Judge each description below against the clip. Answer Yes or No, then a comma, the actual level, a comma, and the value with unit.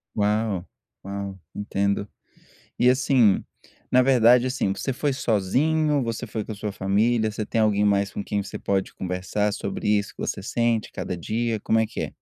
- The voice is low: Yes, low, 105 Hz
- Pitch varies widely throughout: No, average, 3.1 semitones